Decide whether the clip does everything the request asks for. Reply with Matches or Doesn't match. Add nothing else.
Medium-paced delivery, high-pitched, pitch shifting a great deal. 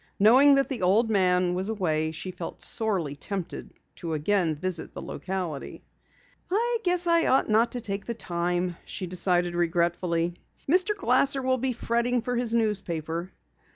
Matches